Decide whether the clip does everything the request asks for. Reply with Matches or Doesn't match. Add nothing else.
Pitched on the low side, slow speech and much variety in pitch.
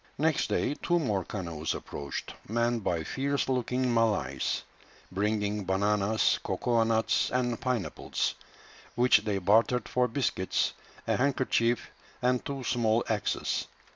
Doesn't match